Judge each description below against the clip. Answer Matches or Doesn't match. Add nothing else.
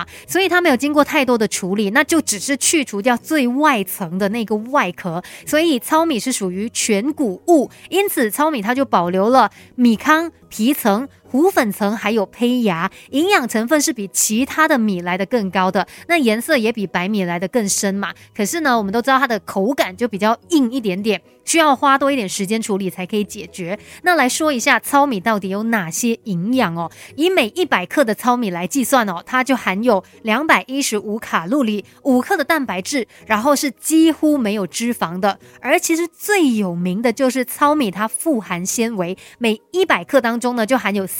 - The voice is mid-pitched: Doesn't match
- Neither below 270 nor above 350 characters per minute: Matches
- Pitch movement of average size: Doesn't match